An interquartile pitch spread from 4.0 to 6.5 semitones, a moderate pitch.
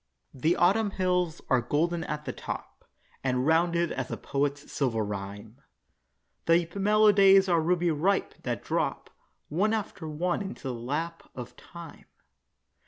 Yes: average, 4.9 semitones; medium, 165 Hz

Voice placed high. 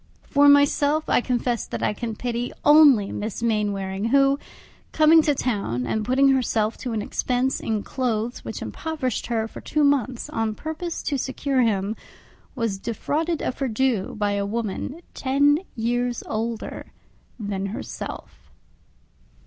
Yes: high, 245 Hz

